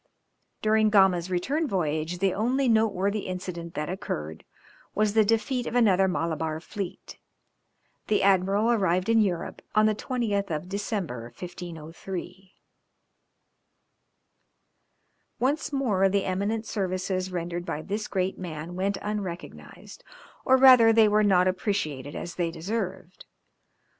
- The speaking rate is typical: No, slow, 125 wpm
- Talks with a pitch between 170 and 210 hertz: Yes, high, 190 Hz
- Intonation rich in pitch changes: No, average, 3.5 semitones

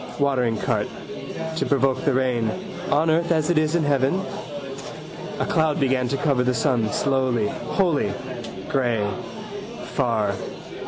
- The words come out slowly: Yes, slow, 130 wpm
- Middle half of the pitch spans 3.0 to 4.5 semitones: Yes, average, 3.6 semitones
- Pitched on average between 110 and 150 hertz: Yes, low, 135 Hz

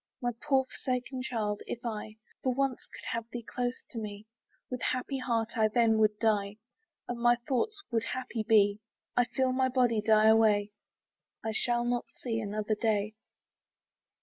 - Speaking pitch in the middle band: No, high, 230 Hz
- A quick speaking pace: No, average, 170 wpm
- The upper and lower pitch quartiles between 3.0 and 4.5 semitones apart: No, narrow, 2.5 semitones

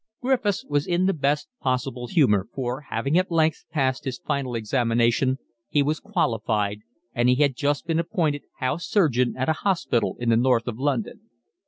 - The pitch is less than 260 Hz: Yes, medium, 140 Hz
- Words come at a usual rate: Yes, average, 175 wpm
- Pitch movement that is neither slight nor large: Yes, average, 4.8 semitones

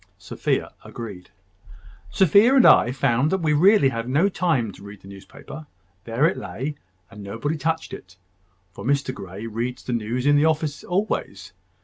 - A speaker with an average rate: Yes, average, 165 wpm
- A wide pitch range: Yes, wide, 5.8 semitones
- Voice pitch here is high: No, low, 135 Hz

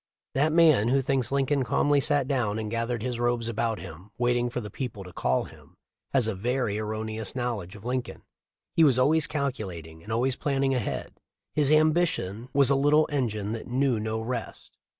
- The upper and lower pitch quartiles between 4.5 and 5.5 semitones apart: No, average, 4.1 semitones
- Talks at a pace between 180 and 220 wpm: Yes, average, 190 wpm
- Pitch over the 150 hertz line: No, low, 120 Hz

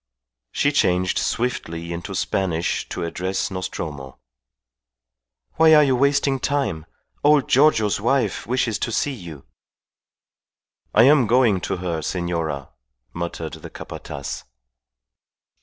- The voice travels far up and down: Yes, wide, 7.8 semitones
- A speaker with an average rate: No, slow, 110 wpm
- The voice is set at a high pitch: No, very low, 95 Hz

